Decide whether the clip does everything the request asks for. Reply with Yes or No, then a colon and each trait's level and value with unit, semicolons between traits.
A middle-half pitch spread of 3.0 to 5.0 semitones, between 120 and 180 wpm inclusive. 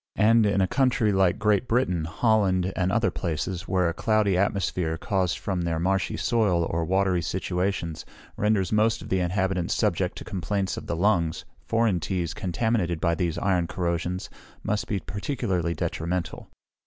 Yes: average, 3.3 semitones; average, 160 wpm